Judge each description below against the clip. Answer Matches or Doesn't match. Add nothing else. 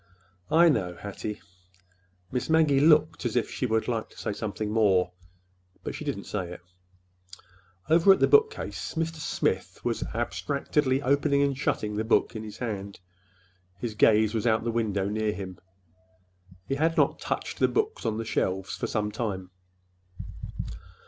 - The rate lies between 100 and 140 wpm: Doesn't match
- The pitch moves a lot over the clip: Matches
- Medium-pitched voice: Doesn't match